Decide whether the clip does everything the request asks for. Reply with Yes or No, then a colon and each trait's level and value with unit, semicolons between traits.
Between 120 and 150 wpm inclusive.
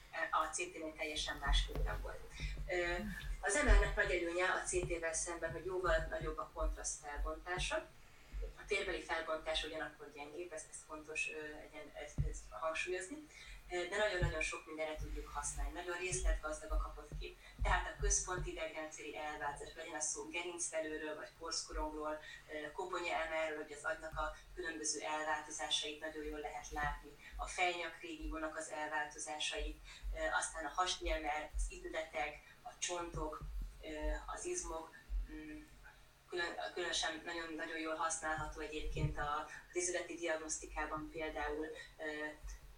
Yes: average, 125 wpm